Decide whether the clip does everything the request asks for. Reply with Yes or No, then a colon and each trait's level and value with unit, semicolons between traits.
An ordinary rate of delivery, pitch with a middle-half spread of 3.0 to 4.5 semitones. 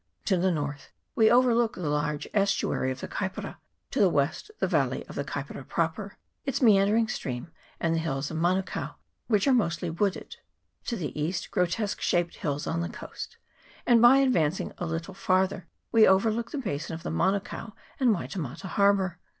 No: average, 175 wpm; average, 4.9 semitones